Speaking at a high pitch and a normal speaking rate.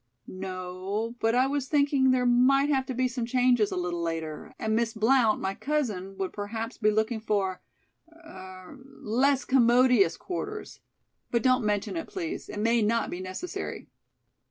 Yes: high, 230 Hz; average, 160 wpm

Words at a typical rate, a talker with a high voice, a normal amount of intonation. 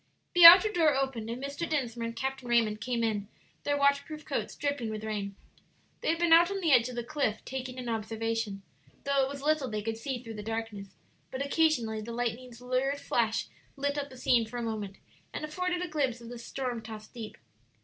No: fast, 210 wpm; very high, 250 Hz; average, 4.0 semitones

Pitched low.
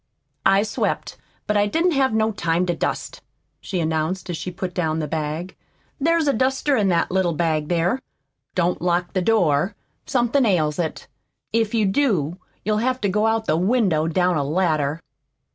No: medium, 185 Hz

